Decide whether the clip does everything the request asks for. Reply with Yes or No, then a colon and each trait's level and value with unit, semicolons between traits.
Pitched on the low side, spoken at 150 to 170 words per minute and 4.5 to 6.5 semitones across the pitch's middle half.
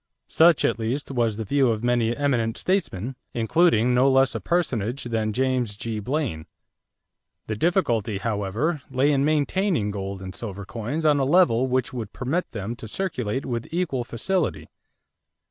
Yes: low, 120 Hz; average, 160 wpm; average, 4.8 semitones